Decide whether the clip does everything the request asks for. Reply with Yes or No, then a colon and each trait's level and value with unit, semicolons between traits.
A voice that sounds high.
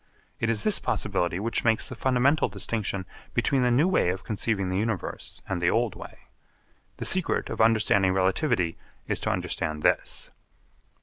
No: low, 110 Hz